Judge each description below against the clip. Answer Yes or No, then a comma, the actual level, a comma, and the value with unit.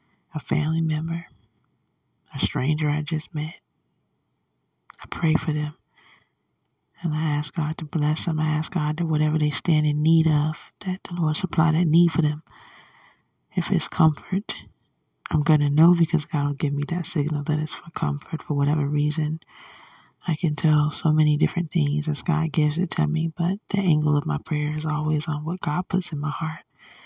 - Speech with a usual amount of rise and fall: No, narrow, 1.6 semitones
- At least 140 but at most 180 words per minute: No, average, 190 wpm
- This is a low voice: No, medium, 155 Hz